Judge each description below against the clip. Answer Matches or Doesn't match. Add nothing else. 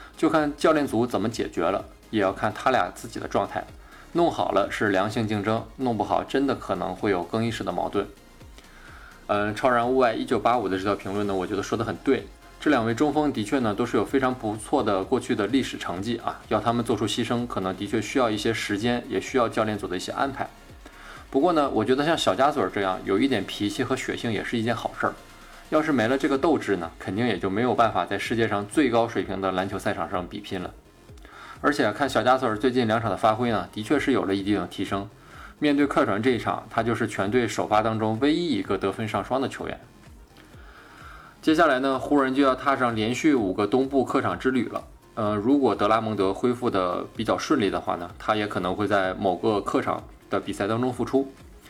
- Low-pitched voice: Matches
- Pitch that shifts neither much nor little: Matches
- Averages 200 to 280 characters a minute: Doesn't match